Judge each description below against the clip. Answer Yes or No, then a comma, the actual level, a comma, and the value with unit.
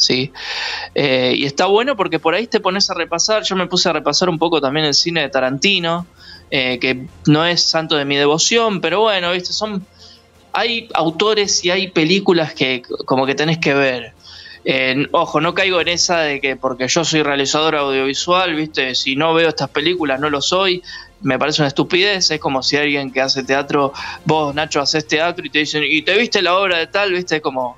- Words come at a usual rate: No, fast, 215 wpm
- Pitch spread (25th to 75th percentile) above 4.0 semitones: Yes, average, 4.4 semitones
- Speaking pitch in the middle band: Yes, medium, 155 Hz